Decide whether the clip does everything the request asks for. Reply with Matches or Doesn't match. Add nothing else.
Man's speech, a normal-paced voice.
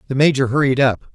Doesn't match